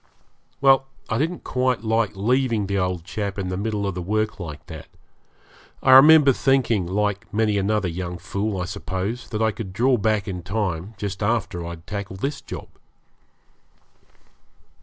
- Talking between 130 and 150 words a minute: No, average, 160 wpm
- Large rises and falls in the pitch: No, average, 3.5 semitones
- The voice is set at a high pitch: No, low, 105 Hz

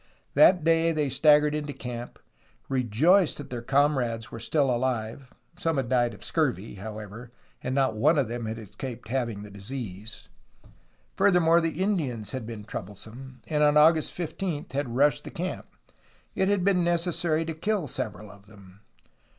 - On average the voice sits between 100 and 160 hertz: Yes, low, 135 Hz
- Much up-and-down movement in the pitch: Yes, wide, 5.9 semitones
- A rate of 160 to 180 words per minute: Yes, average, 165 wpm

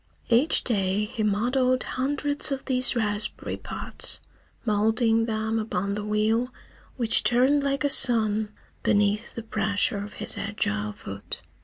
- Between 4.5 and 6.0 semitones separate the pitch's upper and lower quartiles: No, average, 3.3 semitones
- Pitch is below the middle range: No, high, 220 Hz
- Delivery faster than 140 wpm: No, slow, 135 wpm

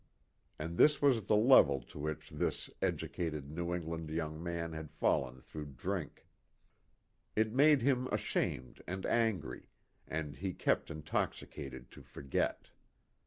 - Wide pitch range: Yes, wide, 5.9 semitones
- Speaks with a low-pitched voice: Yes, very low, 80 Hz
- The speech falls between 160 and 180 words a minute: No, average, 140 wpm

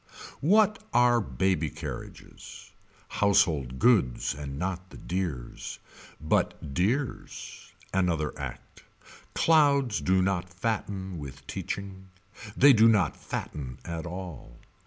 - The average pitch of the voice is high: No, very low, 95 Hz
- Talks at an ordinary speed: No, slow, 105 wpm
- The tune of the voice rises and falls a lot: Yes, wide, 6.3 semitones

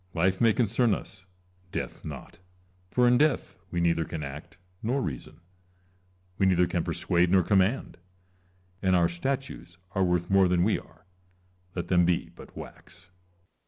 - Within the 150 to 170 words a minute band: Yes, average, 155 wpm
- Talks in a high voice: No, very low, 90 Hz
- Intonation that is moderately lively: Yes, average, 3.1 semitones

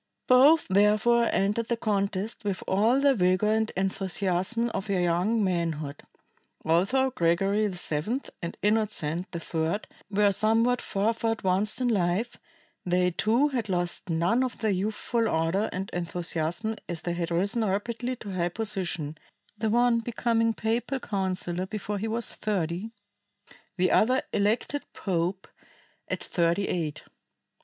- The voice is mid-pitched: No, high, 200 Hz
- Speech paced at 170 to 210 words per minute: No, slow, 135 wpm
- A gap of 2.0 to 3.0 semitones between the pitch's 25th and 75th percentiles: No, average, 4.3 semitones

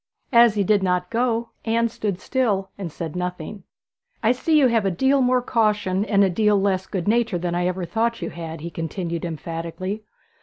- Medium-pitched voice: No, high, 195 Hz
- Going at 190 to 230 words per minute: Yes, average, 195 wpm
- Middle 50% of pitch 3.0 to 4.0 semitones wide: No, average, 4.5 semitones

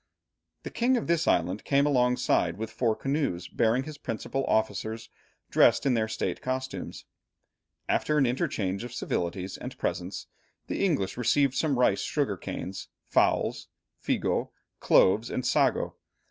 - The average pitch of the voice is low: Yes, low, 125 Hz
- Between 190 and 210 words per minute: No, average, 140 wpm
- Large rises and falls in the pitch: No, average, 4.6 semitones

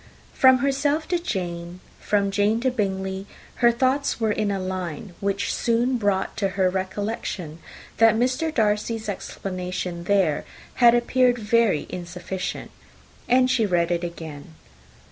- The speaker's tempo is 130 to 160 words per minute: Yes, slow, 135 wpm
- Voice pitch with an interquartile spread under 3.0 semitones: No, average, 4.6 semitones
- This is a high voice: Yes, high, 205 Hz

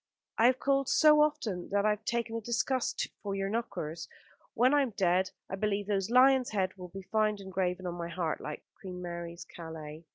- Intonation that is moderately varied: Yes, average, 4.7 semitones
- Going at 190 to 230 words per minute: Yes, average, 200 wpm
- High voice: Yes, high, 195 Hz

